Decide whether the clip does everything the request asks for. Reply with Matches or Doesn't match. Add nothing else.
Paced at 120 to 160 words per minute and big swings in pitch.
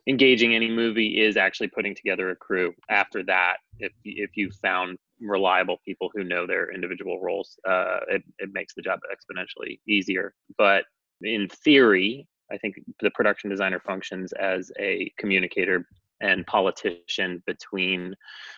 Doesn't match